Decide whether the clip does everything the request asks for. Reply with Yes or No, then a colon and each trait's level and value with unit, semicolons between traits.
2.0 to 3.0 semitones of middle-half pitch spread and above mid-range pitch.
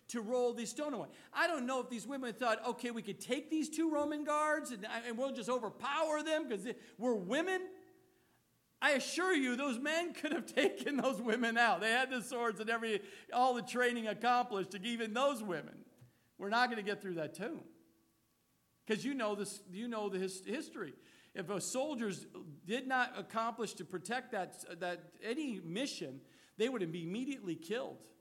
No: average, 4.8 semitones; high, 240 Hz